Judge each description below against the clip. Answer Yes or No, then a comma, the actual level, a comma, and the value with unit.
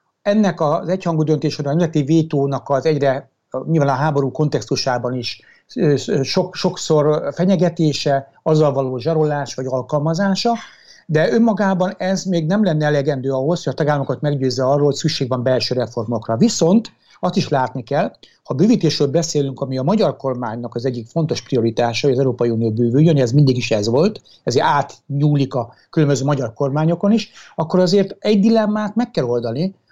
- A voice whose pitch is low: No, medium, 150 Hz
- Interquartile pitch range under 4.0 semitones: No, average, 4.8 semitones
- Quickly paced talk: Yes, fast, 160 wpm